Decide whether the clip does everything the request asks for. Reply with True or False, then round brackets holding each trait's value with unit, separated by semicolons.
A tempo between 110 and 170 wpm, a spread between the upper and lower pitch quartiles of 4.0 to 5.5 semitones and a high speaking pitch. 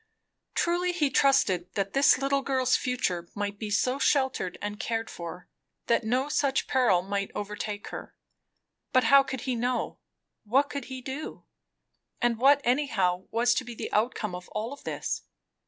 True (160 wpm; 4.7 semitones; 240 Hz)